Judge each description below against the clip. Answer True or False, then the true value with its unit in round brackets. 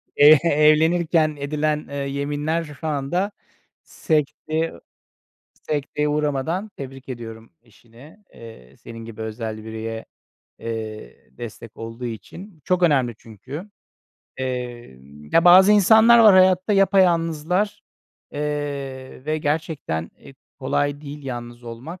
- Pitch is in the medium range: True (145 Hz)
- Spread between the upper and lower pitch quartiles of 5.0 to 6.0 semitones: True (5.5 semitones)